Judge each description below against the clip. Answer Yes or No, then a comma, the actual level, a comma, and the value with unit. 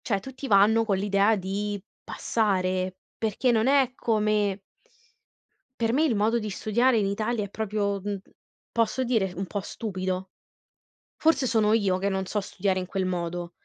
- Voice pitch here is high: Yes, high, 205 Hz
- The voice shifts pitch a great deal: No, average, 2.8 semitones